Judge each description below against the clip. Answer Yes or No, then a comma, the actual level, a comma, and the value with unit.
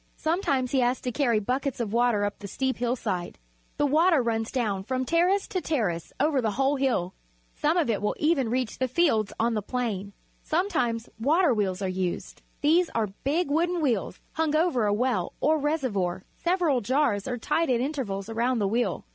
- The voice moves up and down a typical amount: No, wide, 5.9 semitones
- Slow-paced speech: No, average, 190 wpm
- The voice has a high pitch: Yes, very high, 250 Hz